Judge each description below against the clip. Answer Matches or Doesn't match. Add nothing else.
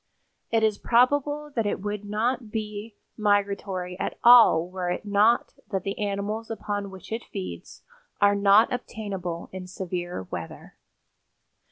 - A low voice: Doesn't match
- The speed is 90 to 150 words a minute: Matches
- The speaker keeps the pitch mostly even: Doesn't match